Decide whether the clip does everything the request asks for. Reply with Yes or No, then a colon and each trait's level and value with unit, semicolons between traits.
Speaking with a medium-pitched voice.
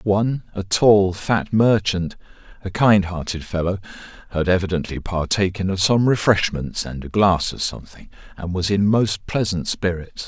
No: very low, 95 Hz